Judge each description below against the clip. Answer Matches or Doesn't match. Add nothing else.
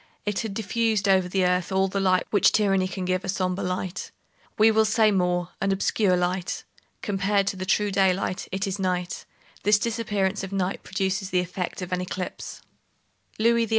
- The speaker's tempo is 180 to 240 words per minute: Matches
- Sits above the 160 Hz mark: Matches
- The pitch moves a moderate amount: Doesn't match